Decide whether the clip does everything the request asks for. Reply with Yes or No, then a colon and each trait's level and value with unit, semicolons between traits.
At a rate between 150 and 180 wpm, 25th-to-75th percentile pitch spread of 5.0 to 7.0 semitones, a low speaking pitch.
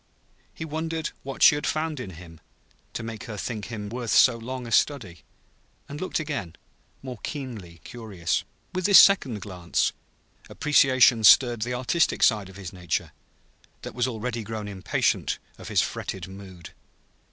Yes: average, 155 wpm; wide, 5.6 semitones; low, 115 Hz